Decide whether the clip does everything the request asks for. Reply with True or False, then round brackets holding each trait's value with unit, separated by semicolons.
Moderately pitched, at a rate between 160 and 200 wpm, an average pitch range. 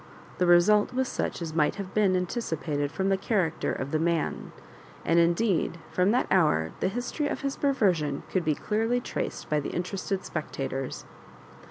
True (180 Hz; 175 wpm; 5.0 semitones)